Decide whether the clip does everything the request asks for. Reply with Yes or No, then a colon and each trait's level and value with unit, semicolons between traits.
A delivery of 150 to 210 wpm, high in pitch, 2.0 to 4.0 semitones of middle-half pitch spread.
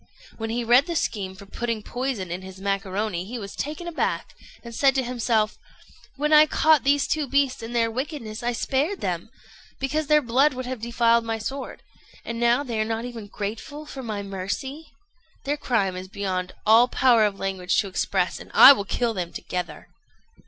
No: average, 190 wpm; high, 235 Hz; average, 5.1 semitones